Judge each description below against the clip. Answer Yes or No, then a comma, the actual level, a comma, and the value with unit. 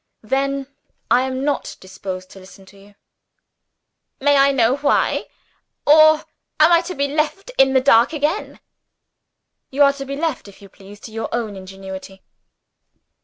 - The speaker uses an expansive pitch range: Yes, wide, 6.3 semitones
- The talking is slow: No, average, 160 wpm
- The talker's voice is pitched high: Yes, very high, 265 Hz